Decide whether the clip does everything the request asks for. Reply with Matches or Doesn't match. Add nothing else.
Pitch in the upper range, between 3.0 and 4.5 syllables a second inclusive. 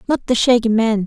Doesn't match